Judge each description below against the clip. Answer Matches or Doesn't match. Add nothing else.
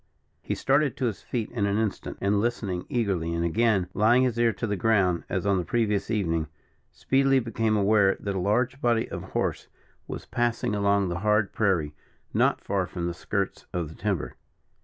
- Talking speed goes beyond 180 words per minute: Matches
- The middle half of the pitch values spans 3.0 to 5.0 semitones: Matches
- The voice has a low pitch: Matches